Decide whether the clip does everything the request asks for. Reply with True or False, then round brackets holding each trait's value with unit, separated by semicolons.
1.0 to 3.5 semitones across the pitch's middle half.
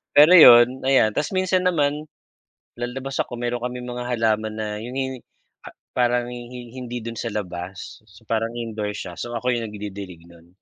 True (2.8 semitones)